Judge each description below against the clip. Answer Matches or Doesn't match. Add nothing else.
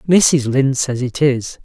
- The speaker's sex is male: Matches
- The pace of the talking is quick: Doesn't match